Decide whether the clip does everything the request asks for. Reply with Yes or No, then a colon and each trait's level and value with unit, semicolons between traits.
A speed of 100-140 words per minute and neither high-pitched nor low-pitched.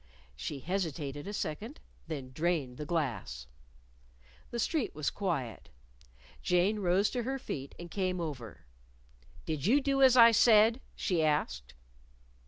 Yes: slow, 135 wpm; medium, 175 Hz